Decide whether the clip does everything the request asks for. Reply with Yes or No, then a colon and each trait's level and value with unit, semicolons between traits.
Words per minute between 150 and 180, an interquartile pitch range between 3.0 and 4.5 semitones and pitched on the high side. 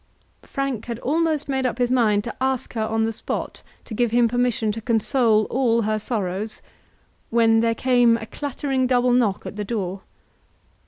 No: average, 175 wpm; narrow, 2.6 semitones; high, 235 Hz